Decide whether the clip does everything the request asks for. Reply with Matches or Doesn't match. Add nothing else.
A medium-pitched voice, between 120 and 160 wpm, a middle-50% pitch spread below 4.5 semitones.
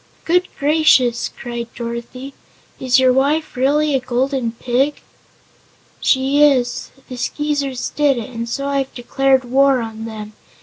Doesn't match